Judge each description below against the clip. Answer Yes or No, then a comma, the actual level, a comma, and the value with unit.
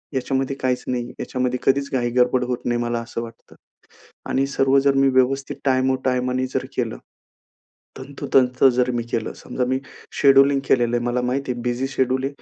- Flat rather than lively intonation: Yes, narrow, 1.5 semitones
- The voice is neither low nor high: No, low, 130 Hz